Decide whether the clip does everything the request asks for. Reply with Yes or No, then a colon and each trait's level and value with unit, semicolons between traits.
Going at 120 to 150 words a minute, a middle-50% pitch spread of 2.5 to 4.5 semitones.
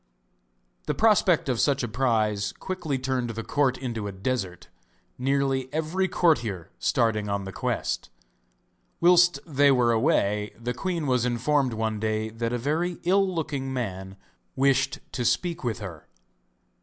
No: average, 145 wpm; average, 5.1 semitones